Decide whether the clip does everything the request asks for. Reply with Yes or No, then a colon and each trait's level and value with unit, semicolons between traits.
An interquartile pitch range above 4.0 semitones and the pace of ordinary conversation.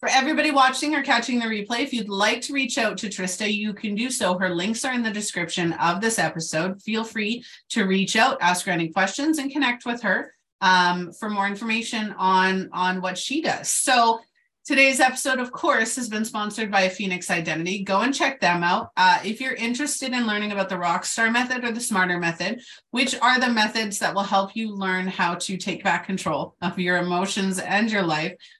No: average, 4.7 semitones; fast, 210 wpm